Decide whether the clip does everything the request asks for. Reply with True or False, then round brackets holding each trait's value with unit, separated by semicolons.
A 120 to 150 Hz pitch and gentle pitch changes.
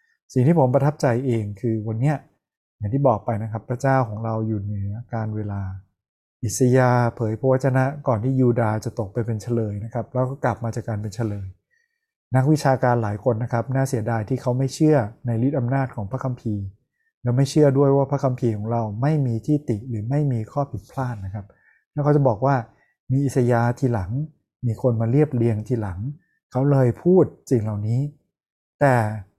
False (125 Hz; 3.3 semitones)